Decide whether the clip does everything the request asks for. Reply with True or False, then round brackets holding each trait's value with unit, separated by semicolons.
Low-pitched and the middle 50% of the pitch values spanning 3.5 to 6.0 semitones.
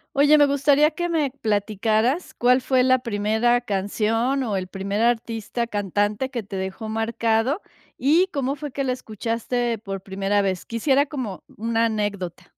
False (230 Hz; 4.4 semitones)